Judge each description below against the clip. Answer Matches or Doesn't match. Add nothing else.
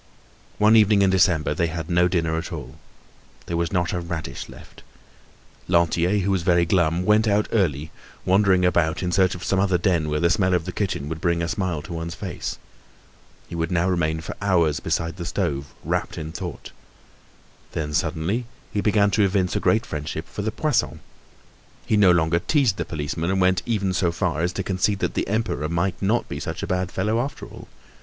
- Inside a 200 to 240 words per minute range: Matches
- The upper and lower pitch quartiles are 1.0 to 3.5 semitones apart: Matches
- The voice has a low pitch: Matches